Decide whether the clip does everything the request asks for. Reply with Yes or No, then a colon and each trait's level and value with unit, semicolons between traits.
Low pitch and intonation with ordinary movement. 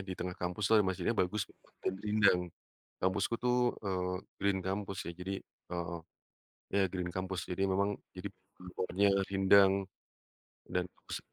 No: very low, 95 Hz; narrow, 1.6 semitones